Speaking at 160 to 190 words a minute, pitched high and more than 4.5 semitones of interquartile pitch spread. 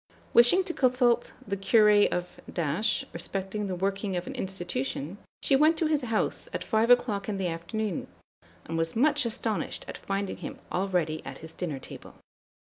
Yes: average, 165 wpm; high, 200 Hz; average, 4.9 semitones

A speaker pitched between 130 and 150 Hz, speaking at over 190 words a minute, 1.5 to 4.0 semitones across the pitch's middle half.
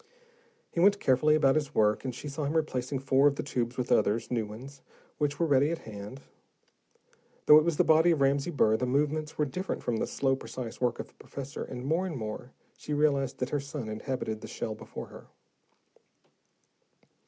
Yes: low, 135 Hz; average, 200 wpm; average, 3.5 semitones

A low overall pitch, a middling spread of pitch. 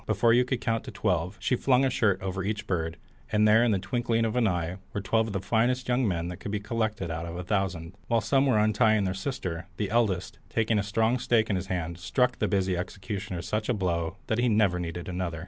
Yes: low, 105 Hz; average, 3.9 semitones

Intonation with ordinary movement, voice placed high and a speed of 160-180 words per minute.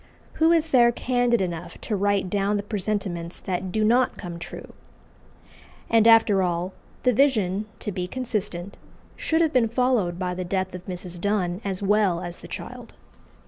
Yes: average, 4.2 semitones; high, 200 Hz; average, 170 wpm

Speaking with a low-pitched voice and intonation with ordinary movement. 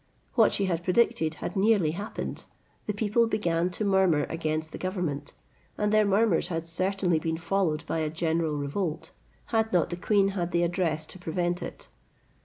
No: medium, 175 Hz; average, 3.5 semitones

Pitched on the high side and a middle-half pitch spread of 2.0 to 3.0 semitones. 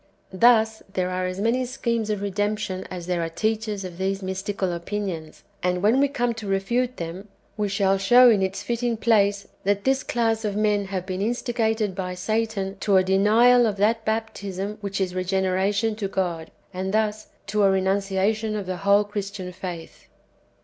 Yes: high, 200 Hz; narrow, 2.6 semitones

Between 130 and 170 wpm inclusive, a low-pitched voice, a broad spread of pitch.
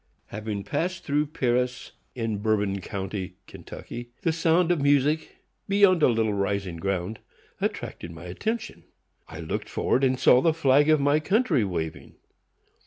Yes: average, 145 wpm; low, 125 Hz; wide, 7.7 semitones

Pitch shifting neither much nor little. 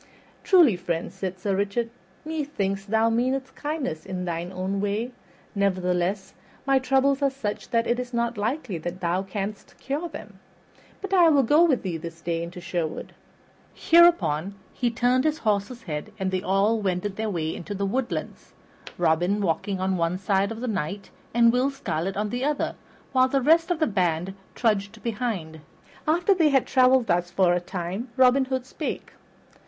No: wide, 5.9 semitones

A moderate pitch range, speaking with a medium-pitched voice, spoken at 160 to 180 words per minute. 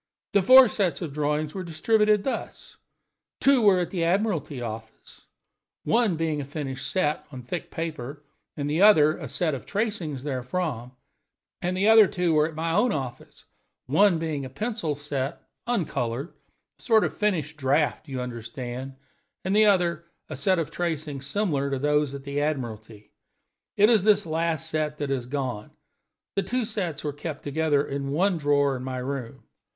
Yes: average, 5.0 semitones; medium, 155 Hz; average, 170 wpm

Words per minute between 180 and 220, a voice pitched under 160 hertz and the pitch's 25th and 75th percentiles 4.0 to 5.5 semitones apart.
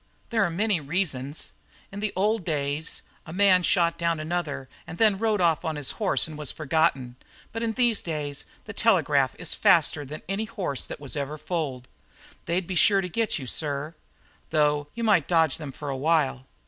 No: average, 190 wpm; medium, 165 Hz; average, 5.0 semitones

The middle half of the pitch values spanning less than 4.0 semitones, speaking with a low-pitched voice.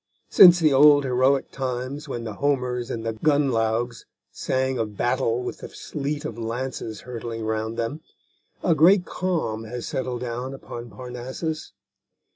Yes: average, 3.6 semitones; low, 125 Hz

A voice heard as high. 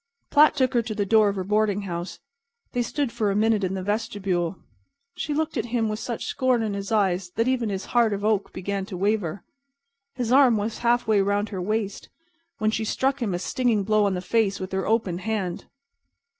Yes: high, 215 Hz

